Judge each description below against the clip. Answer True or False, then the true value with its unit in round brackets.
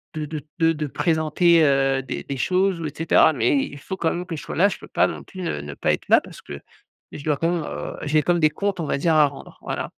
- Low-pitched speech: False (155 Hz)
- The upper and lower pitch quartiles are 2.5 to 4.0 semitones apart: True (3.3 semitones)